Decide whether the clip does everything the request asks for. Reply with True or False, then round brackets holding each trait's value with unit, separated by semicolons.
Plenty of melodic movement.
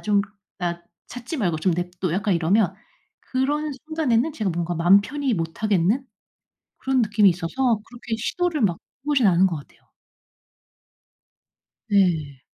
True (6.8 semitones)